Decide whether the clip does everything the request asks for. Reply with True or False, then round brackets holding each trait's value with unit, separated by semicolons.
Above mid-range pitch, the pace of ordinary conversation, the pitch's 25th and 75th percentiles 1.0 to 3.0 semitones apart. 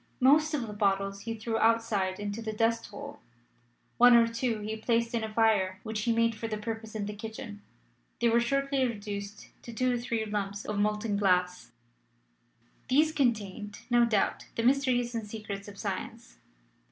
True (220 Hz; 175 wpm; 2.4 semitones)